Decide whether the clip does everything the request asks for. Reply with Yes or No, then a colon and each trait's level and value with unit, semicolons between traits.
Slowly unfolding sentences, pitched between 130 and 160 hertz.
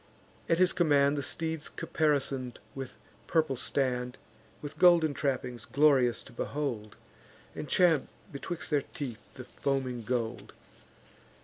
Yes: slow, 120 wpm; medium, 140 Hz